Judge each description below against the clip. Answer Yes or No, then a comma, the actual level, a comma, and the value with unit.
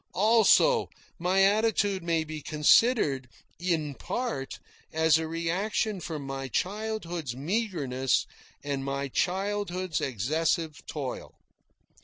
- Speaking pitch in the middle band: Yes, medium, 165 Hz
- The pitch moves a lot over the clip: Yes, wide, 5.9 semitones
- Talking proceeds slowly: Yes, slow, 100 wpm